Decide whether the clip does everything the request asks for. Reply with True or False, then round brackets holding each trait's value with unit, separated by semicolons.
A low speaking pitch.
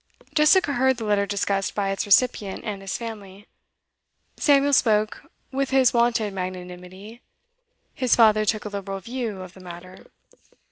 False (210 Hz)